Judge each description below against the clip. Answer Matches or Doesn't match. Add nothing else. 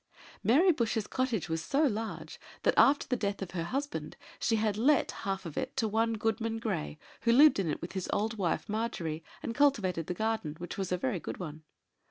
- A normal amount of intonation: Matches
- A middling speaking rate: Doesn't match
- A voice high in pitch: Matches